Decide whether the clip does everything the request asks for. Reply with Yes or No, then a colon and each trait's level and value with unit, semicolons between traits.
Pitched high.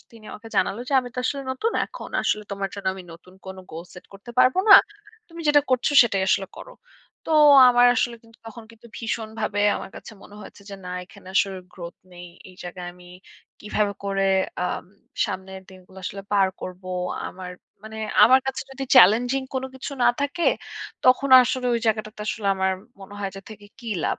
Yes: high, 210 Hz